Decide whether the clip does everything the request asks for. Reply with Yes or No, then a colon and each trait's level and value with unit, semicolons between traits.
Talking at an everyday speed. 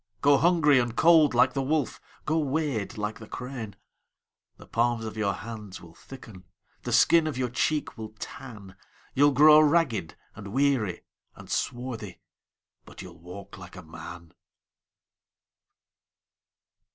No: slow, 130 wpm